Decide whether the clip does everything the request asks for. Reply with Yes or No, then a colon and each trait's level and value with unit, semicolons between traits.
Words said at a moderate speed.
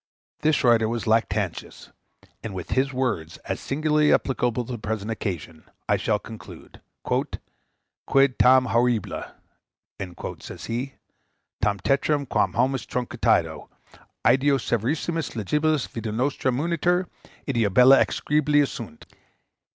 No: slow, 115 wpm